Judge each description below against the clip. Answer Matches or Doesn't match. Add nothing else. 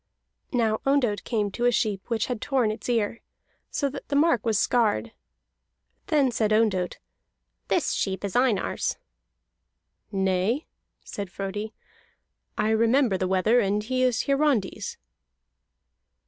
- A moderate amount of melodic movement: Matches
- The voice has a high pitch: Matches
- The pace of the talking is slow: Matches